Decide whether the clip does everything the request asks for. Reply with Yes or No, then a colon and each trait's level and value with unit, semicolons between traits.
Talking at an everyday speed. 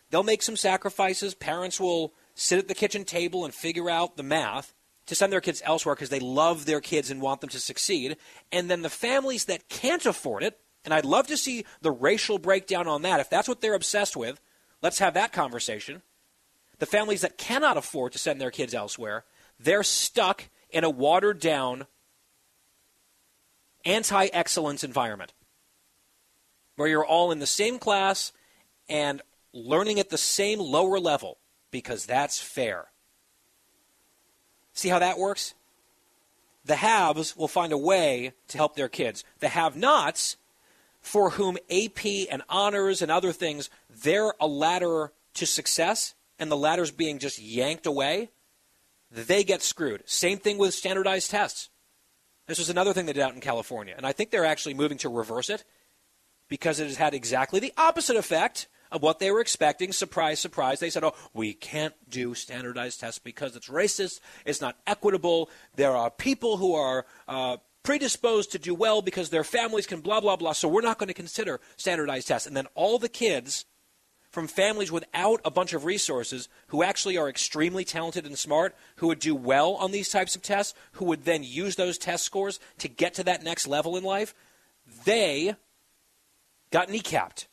Yes: average, 175 wpm